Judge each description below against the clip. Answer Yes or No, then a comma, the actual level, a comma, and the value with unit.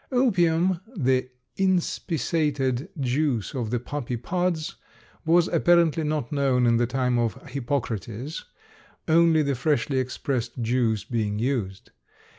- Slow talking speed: Yes, slow, 115 wpm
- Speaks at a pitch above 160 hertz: No, low, 135 Hz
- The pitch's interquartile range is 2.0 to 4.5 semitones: No, average, 5.1 semitones